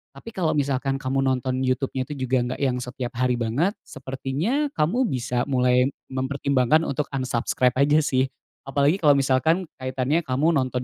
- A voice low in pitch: Yes, low, 130 Hz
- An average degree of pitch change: No, narrow, 2.1 semitones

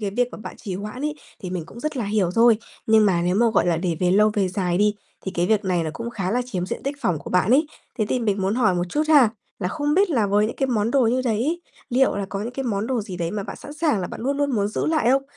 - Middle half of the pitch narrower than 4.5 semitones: No, average, 5.0 semitones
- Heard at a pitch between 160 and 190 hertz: No, high, 215 Hz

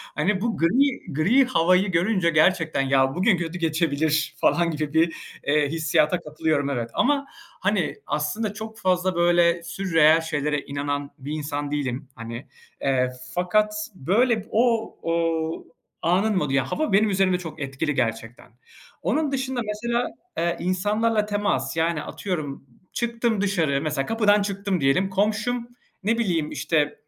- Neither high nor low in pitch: Yes, medium, 170 Hz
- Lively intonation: Yes, wide, 5.7 semitones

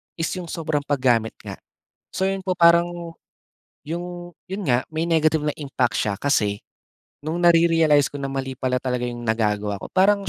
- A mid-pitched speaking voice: Yes, medium, 155 Hz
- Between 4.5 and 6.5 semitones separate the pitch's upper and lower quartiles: Yes, average, 5.2 semitones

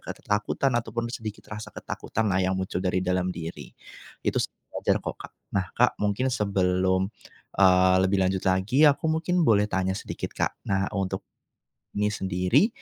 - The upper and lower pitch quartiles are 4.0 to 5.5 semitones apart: No, average, 2.7 semitones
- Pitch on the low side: Yes, very low, 95 Hz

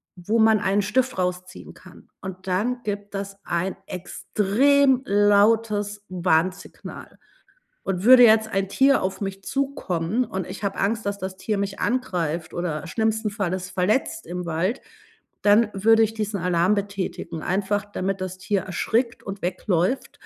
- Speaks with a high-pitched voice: Yes, high, 200 Hz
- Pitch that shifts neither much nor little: Yes, average, 3.1 semitones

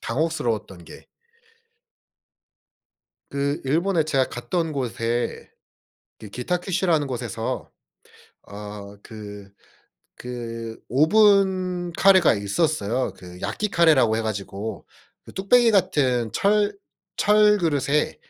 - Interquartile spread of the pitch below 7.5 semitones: No, wide, 8.1 semitones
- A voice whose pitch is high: No, medium, 140 Hz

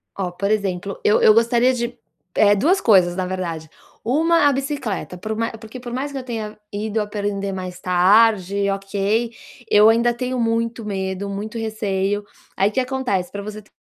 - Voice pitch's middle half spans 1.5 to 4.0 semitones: Yes, average, 3.2 semitones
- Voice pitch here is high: Yes, high, 210 Hz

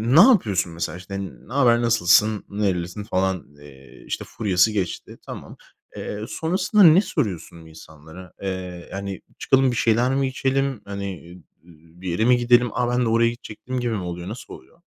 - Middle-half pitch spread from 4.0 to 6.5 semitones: Yes, wide, 5.5 semitones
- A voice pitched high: No, low, 105 Hz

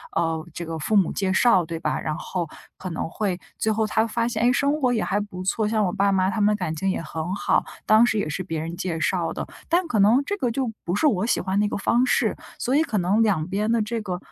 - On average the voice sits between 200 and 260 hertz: Yes, high, 205 Hz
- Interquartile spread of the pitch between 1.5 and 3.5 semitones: No, average, 4.2 semitones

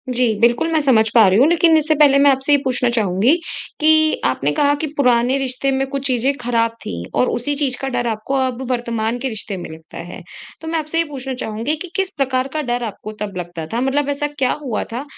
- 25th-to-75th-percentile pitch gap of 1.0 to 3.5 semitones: No, average, 3.9 semitones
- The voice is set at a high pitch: Yes, very high, 255 Hz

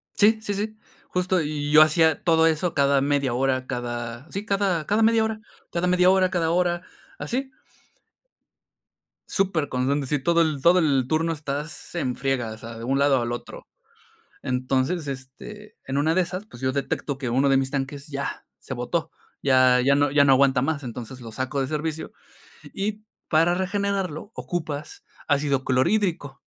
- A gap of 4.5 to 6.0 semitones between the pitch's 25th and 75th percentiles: Yes, average, 5.1 semitones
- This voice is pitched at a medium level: Yes, medium, 145 Hz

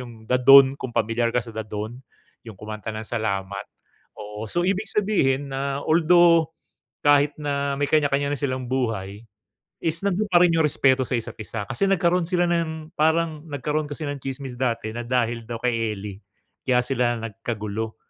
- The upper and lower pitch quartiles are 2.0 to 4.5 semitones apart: No, wide, 5.6 semitones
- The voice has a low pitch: Yes, low, 130 Hz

